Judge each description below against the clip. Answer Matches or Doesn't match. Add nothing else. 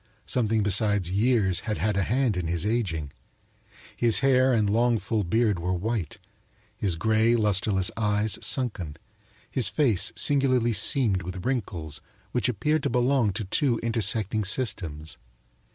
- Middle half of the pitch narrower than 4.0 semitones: Doesn't match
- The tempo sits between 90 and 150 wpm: Matches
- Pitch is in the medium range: Doesn't match